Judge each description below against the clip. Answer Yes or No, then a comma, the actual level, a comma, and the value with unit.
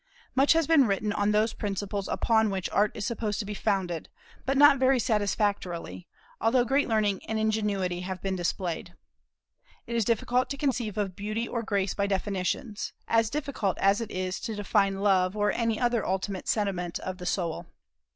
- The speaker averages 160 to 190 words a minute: Yes, average, 180 wpm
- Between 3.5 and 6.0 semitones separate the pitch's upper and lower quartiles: No, average, 3.0 semitones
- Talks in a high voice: Yes, high, 205 Hz